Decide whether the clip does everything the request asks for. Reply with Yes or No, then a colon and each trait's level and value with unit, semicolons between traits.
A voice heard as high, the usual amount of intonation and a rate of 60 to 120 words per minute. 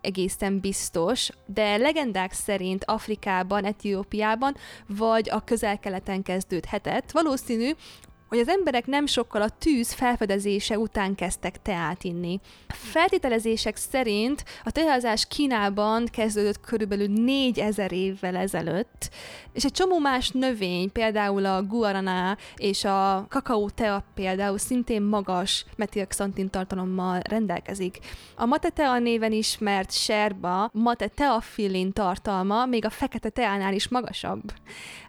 Yes: high, 210 Hz; average, 3.5 semitones; average, 115 wpm